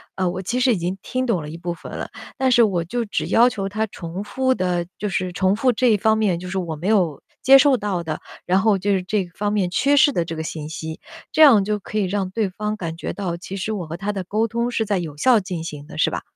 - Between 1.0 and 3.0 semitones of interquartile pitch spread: No, average, 3.9 semitones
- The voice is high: Yes, high, 195 Hz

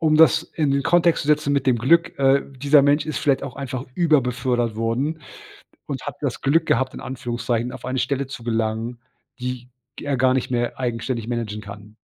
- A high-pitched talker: No, low, 130 Hz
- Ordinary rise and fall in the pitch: Yes, average, 3.1 semitones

